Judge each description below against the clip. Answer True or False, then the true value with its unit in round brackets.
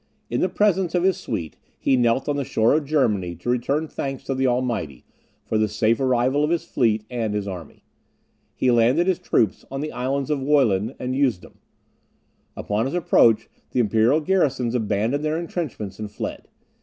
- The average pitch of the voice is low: True (125 Hz)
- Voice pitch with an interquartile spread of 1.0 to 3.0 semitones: False (5.0 semitones)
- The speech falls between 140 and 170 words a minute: False (180 wpm)